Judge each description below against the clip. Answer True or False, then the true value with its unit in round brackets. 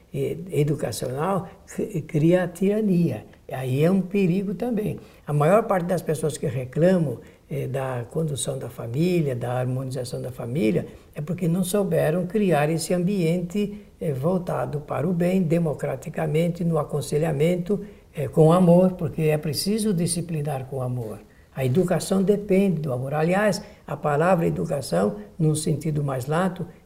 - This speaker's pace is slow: False (140 wpm)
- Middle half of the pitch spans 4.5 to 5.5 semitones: False (4.1 semitones)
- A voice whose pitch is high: False (160 Hz)